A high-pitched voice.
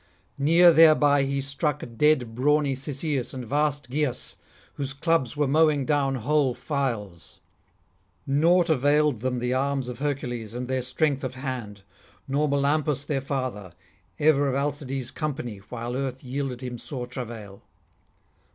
No: low, 135 Hz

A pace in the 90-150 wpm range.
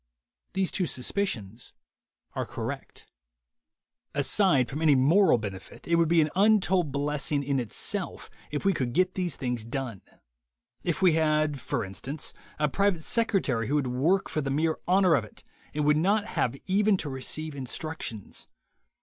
No: average, 160 wpm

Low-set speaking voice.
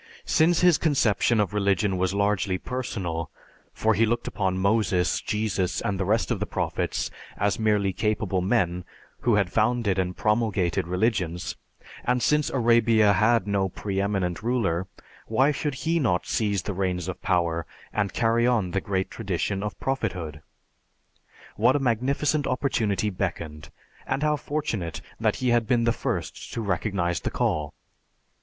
Yes: low, 105 Hz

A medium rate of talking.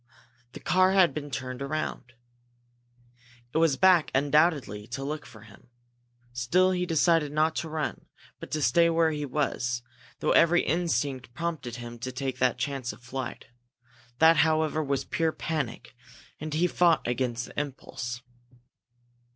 Yes: average, 150 wpm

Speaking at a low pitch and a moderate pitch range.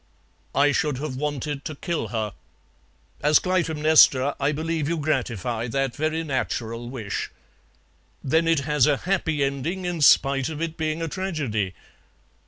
No: medium, 150 Hz; average, 3.3 semitones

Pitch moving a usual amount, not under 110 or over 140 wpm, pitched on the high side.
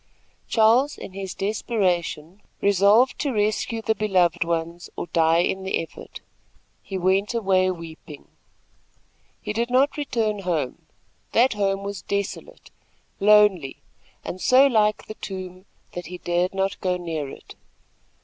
Yes: average, 3.3 semitones; slow, 135 wpm; high, 195 Hz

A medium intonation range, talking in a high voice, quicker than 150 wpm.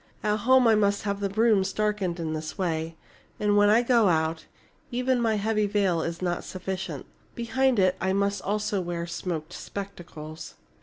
Yes: average, 3.6 semitones; high, 200 Hz; average, 170 wpm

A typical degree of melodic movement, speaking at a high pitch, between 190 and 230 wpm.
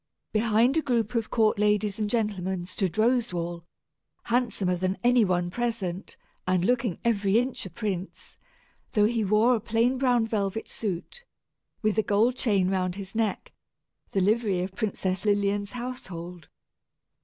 No: average, 3.7 semitones; high, 210 Hz; average, 145 wpm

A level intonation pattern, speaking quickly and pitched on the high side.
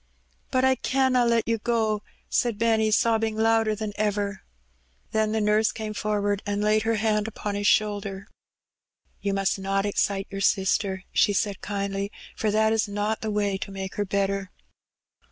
No: narrow, 1.6 semitones; average, 170 wpm; high, 210 Hz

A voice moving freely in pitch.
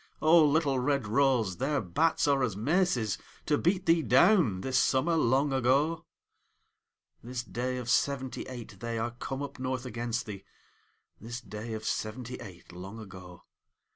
No: average, 4.1 semitones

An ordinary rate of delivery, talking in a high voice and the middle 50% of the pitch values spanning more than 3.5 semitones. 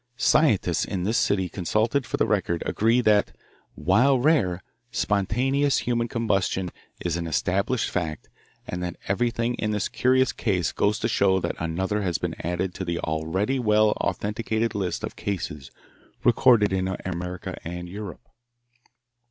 No: average, 145 wpm; low, 100 Hz; average, 4.5 semitones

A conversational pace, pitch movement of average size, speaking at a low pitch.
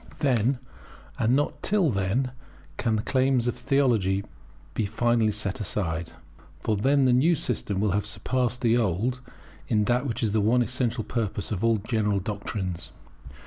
Yes: average, 160 wpm; average, 3.5 semitones; low, 115 Hz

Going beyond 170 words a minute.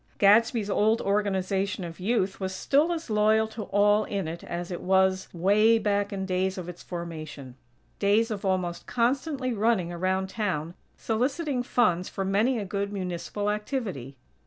No: average, 160 wpm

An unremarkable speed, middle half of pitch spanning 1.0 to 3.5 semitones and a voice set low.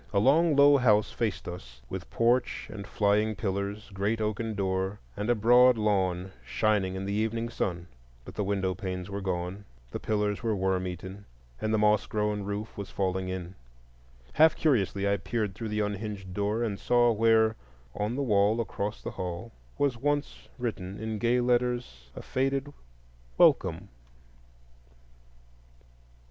Yes: average, 155 wpm; average, 3.1 semitones; low, 105 Hz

